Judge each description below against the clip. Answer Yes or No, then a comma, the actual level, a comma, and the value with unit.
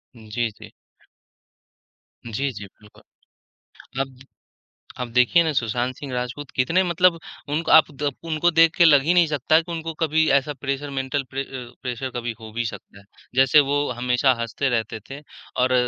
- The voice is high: No, low, 135 Hz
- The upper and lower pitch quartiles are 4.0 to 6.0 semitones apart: Yes, average, 4.3 semitones